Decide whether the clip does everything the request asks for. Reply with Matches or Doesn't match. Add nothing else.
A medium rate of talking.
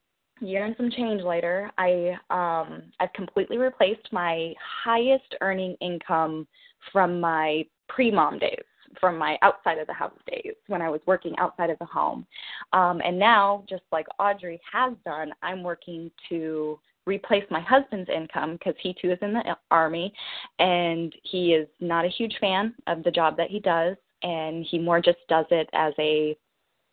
Matches